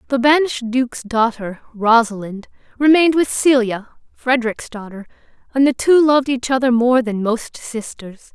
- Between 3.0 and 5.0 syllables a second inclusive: Yes, 4.9 syllables/s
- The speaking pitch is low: No, high, 245 Hz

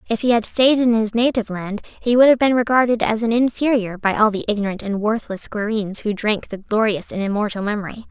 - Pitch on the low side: No, high, 220 Hz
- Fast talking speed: Yes, fast, 220 wpm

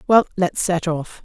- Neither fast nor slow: Yes, average, 195 wpm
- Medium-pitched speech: Yes, medium, 175 Hz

